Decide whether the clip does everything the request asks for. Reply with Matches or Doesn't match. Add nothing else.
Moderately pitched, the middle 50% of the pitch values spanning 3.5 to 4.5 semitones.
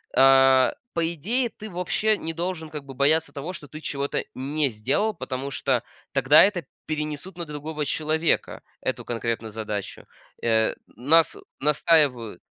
Matches